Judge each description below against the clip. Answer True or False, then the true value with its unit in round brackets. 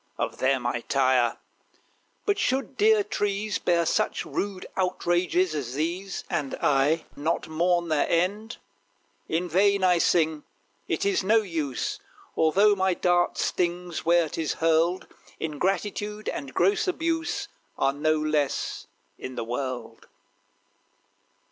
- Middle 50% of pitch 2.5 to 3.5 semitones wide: False (4.5 semitones)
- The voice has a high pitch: False (170 Hz)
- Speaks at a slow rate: True (125 wpm)